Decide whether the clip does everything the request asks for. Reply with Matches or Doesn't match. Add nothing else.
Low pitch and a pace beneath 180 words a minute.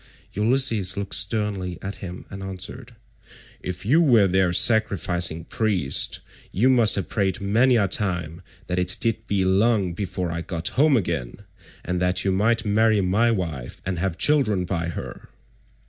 Matches